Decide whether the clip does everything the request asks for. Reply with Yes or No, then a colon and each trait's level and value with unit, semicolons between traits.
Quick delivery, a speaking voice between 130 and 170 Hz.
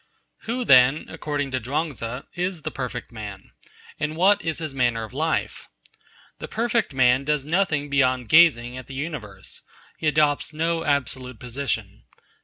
No: average, 155 wpm; medium, 140 Hz